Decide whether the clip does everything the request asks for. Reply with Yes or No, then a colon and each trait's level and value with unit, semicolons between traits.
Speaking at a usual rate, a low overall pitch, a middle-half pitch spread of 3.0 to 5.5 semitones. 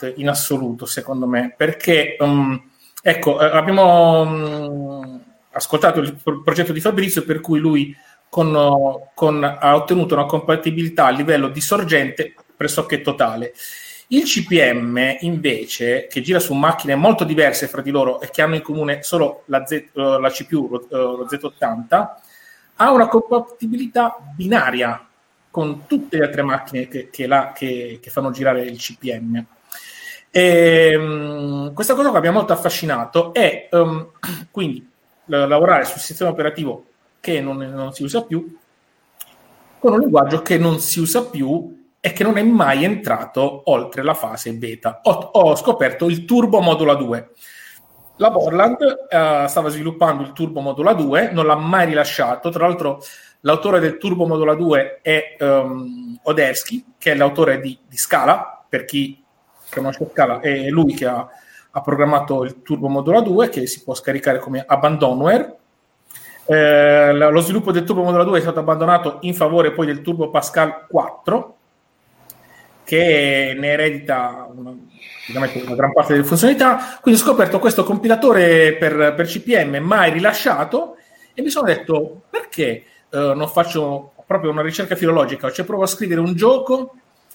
No: average, 150 wpm; medium, 155 Hz; average, 4.1 semitones